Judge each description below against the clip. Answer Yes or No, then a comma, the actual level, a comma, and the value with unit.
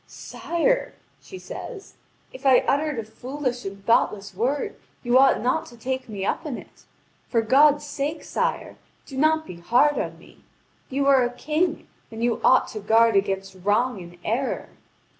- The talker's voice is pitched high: Yes, very high, 255 Hz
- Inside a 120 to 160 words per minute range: No, average, 170 wpm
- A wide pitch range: No, average, 4.9 semitones